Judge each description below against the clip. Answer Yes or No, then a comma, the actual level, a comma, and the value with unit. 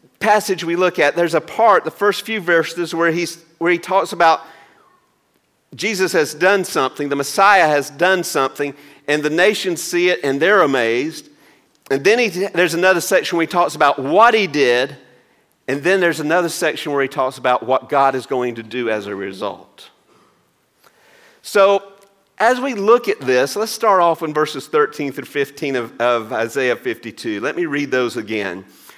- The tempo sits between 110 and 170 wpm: No, average, 180 wpm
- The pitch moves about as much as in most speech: No, wide, 5.9 semitones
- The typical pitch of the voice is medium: Yes, medium, 170 Hz